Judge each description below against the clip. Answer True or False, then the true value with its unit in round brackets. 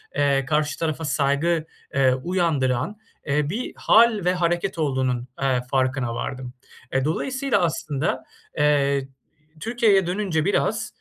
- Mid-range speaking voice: True (150 Hz)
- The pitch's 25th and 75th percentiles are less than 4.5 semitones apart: False (5.0 semitones)